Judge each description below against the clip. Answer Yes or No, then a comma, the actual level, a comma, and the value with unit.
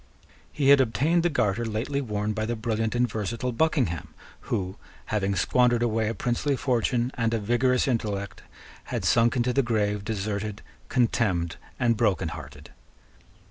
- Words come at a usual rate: Yes, average, 150 wpm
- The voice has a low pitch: Yes, low, 115 Hz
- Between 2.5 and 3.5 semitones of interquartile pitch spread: Yes, average, 2.9 semitones